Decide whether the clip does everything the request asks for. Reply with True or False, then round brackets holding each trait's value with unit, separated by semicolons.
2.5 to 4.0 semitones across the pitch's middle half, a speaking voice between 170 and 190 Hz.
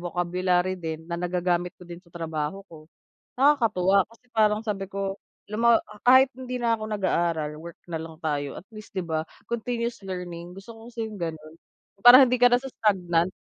False (4.6 semitones; 185 Hz)